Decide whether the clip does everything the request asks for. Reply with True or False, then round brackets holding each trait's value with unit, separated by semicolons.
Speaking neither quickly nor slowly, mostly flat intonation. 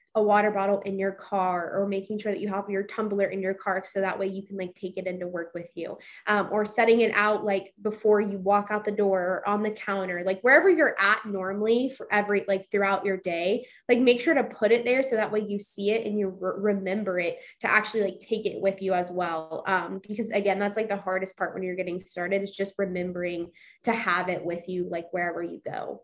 False (245 wpm; 2.2 semitones)